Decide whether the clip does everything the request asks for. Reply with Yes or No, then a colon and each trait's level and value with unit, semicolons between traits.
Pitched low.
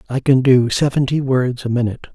Yes: low, 130 Hz